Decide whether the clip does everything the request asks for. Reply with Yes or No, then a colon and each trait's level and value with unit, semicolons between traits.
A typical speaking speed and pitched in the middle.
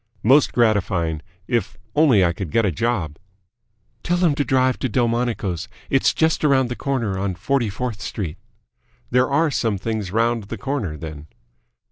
No: average, 160 wpm; low, 115 Hz